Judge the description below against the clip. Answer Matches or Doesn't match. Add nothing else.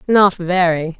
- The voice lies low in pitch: Doesn't match